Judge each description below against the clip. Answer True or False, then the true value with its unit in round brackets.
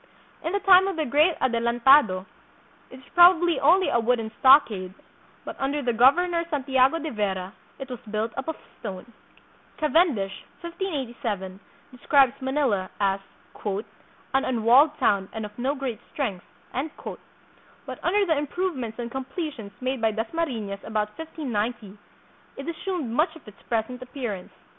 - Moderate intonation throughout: False (5.9 semitones)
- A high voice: True (255 Hz)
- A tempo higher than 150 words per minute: False (145 wpm)